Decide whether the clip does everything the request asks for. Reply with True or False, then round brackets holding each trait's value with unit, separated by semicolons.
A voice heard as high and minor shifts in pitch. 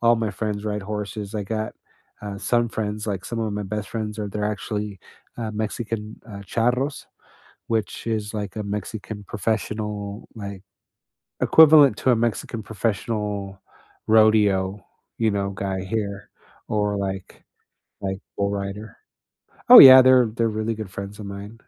False (105 Hz; 1.8 semitones)